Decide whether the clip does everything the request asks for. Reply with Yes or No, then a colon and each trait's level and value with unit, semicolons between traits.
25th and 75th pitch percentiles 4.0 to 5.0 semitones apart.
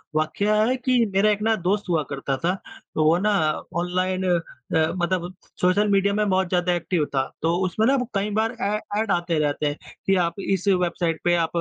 No: average, 3.2 semitones